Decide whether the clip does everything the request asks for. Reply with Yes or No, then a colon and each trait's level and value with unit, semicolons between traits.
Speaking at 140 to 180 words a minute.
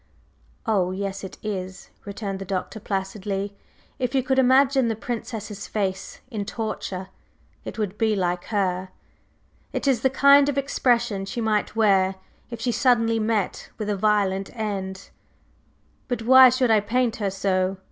Yes: average, 155 wpm